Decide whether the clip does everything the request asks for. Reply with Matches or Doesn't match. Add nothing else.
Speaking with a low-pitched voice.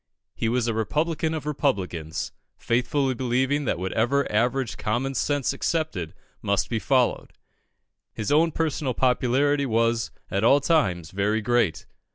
Matches